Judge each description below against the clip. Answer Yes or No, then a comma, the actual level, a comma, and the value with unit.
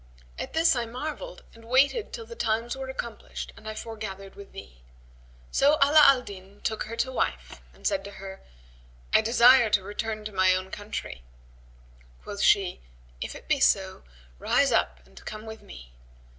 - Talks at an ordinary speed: Yes, average, 175 wpm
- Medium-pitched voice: No, high, 220 Hz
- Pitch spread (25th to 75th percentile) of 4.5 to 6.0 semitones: Yes, average, 4.9 semitones